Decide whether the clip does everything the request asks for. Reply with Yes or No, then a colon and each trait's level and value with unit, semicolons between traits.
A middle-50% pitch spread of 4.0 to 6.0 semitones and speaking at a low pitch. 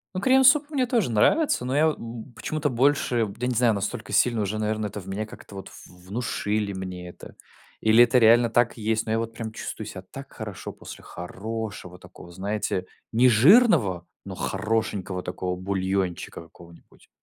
Yes: average, 4.3 semitones; low, 110 Hz